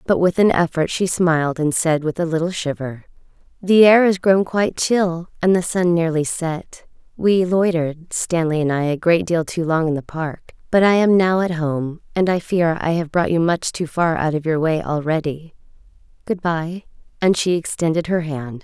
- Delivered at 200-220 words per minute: Yes, fast, 205 wpm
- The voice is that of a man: No, female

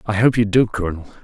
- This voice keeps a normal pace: No, fast, 245 wpm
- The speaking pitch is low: Yes, low, 105 Hz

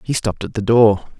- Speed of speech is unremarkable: No, fast, 250 wpm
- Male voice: Yes, male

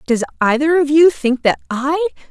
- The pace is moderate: Yes, average, 180 wpm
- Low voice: No, very high, 290 Hz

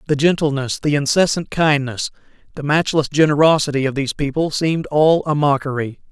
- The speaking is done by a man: Yes, male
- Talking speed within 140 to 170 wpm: Yes, average, 145 wpm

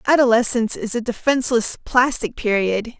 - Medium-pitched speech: No, high, 235 Hz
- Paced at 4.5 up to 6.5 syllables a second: Yes, 5.3 syllables/s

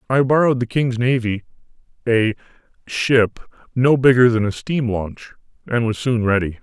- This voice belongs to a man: Yes, male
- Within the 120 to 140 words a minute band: Yes, slow, 135 wpm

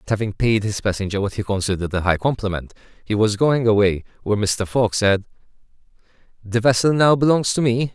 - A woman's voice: No, male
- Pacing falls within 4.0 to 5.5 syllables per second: No, 5.9 syllables/s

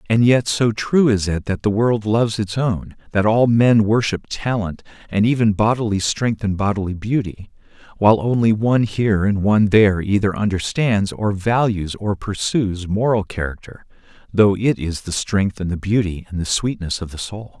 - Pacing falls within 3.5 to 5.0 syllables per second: Yes, 4.9 syllables/s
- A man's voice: Yes, male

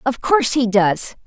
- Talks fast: No, average, 190 wpm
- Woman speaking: Yes, female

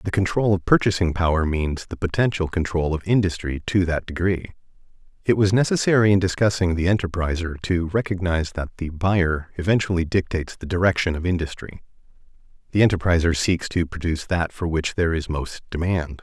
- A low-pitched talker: Yes, very low, 90 Hz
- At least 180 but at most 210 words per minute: No, average, 165 wpm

